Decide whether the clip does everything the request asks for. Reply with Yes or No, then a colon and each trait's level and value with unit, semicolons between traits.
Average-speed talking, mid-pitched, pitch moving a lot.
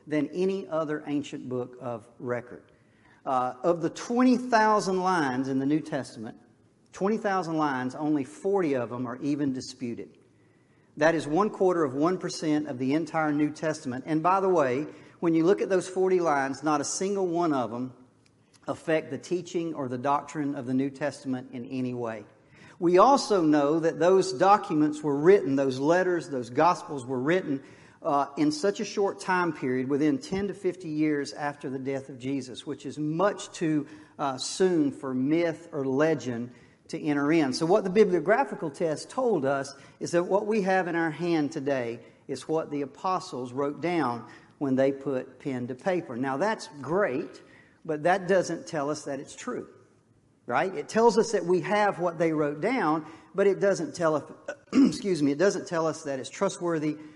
No: average, 190 wpm; medium, 155 Hz; average, 5.0 semitones